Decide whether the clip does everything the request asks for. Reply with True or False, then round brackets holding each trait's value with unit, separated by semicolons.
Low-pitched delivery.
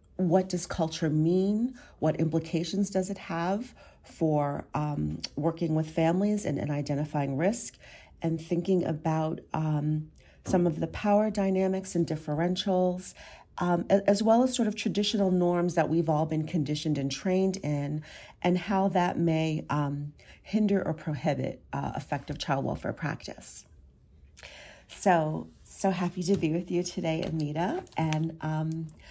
False (165 Hz)